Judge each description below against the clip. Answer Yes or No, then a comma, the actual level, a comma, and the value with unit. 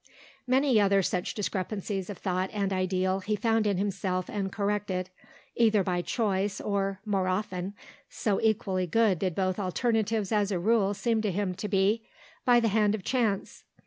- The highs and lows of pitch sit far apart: No, narrow, 2.4 semitones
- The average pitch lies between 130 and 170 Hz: No, high, 200 Hz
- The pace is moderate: Yes, average, 170 wpm